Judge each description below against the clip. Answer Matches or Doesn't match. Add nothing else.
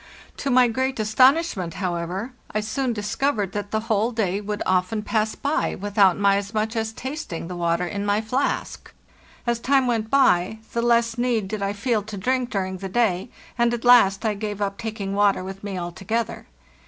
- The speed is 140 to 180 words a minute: Doesn't match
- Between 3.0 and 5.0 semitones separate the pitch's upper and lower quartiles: Matches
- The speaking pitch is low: Doesn't match